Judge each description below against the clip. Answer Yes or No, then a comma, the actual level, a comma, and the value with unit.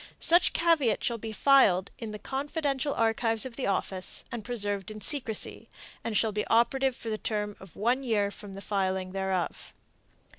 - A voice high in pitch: Yes, high, 220 Hz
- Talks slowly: No, average, 175 wpm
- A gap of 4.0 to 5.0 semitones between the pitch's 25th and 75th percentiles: Yes, average, 4.4 semitones